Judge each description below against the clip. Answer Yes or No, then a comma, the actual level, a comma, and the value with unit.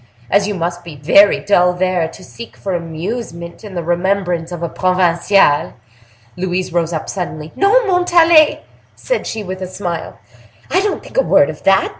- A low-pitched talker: No, medium, 185 Hz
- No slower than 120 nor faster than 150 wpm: No, average, 175 wpm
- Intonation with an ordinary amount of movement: Yes, average, 3.3 semitones